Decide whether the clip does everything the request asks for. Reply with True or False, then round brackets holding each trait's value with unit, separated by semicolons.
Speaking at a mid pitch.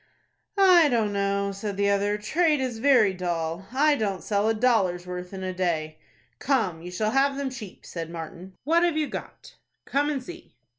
False (205 Hz)